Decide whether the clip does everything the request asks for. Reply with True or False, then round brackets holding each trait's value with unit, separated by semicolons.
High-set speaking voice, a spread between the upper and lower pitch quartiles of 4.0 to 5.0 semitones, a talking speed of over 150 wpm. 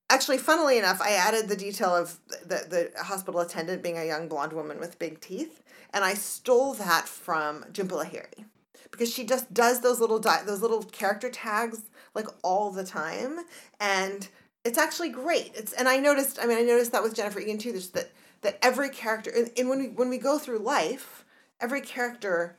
True (225 Hz; 4.7 semitones; 195 wpm)